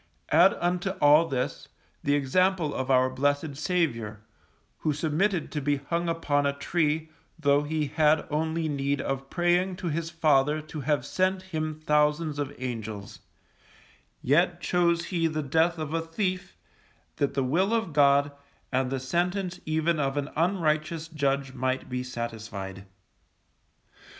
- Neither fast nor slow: Yes, average, 145 wpm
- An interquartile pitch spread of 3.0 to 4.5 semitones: Yes, average, 3.4 semitones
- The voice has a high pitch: No, medium, 150 Hz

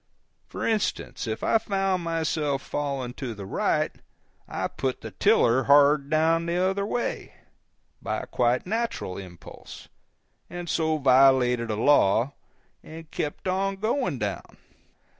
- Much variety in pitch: Yes, wide, 6.3 semitones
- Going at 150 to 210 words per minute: No, slow, 135 wpm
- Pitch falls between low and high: Yes, medium, 145 Hz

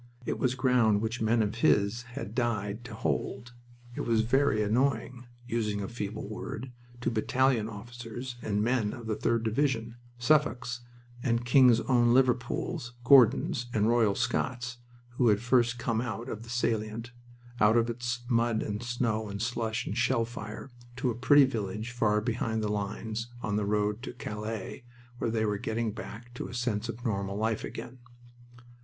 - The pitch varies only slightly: Yes, narrow, 2.2 semitones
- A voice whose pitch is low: Yes, low, 115 Hz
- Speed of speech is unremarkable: Yes, average, 170 wpm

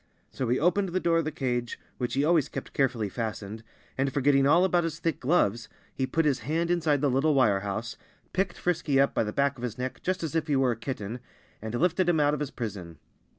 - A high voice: No, medium, 140 Hz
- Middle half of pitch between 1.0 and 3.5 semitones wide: No, average, 5.3 semitones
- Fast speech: Yes, fast, 240 wpm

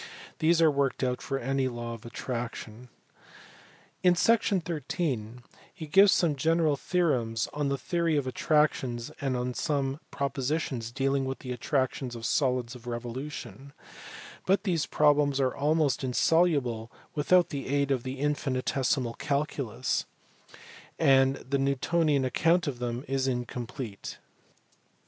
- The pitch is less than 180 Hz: Yes, low, 135 Hz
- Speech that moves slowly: Yes, slow, 130 wpm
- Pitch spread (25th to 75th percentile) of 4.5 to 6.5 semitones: No, average, 3.3 semitones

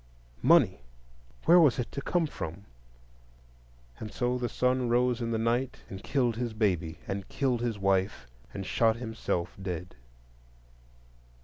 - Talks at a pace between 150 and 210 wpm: No, average, 140 wpm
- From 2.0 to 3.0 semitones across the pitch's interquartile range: No, average, 4.2 semitones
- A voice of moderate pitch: No, low, 115 Hz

